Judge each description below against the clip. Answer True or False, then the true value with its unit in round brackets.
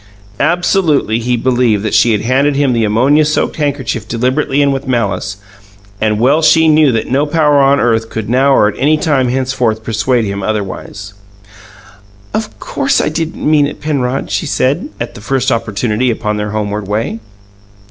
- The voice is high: False (125 Hz)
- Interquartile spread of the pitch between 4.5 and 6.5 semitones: True (4.8 semitones)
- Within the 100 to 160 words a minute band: False (175 wpm)